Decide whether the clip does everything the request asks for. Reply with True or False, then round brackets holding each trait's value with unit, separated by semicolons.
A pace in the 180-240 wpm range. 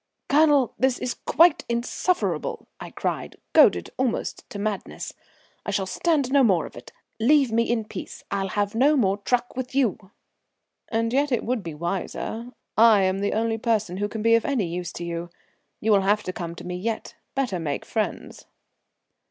True (185 wpm)